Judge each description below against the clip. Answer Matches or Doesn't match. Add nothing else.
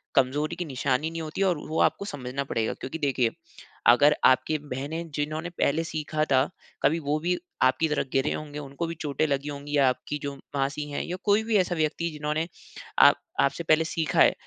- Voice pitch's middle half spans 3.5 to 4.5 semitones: Doesn't match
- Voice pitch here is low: Doesn't match